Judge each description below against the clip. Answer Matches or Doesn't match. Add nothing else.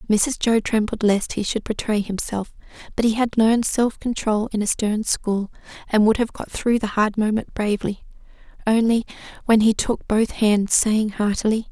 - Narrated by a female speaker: Matches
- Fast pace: Doesn't match